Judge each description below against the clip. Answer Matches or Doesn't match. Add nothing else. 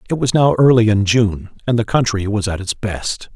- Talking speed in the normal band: Doesn't match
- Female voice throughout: Doesn't match